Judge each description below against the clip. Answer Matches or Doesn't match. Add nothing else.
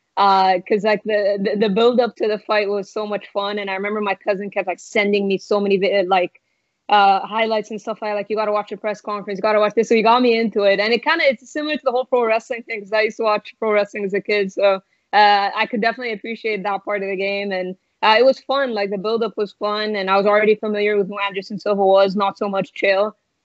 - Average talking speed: Doesn't match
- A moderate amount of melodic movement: Doesn't match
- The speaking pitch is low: Doesn't match